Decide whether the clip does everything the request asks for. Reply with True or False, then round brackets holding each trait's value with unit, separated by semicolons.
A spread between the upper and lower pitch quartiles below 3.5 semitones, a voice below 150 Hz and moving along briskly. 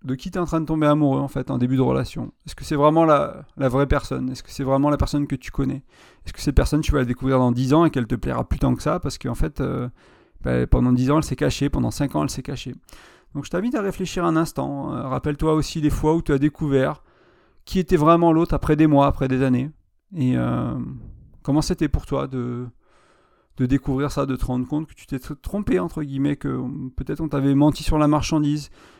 True (2.7 semitones; 140 Hz; 250 wpm)